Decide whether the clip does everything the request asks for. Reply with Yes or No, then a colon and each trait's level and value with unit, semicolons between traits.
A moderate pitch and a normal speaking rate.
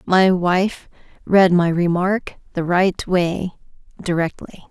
No: medium, 180 Hz; slow, 115 wpm